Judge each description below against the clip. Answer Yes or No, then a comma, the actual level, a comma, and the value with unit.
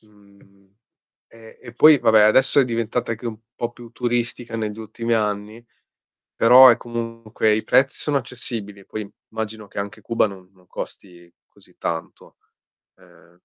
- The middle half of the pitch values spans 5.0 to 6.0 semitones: No, narrow, 2.5 semitones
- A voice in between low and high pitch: No, low, 110 Hz